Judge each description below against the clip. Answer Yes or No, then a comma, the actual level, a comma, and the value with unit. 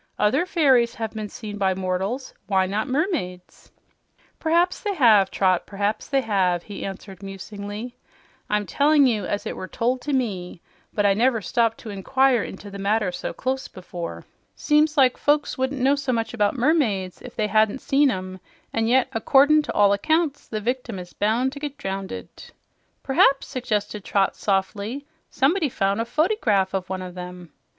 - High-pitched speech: Yes, high, 220 Hz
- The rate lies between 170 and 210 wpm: Yes, average, 175 wpm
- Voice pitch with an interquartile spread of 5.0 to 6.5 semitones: Yes, wide, 5.4 semitones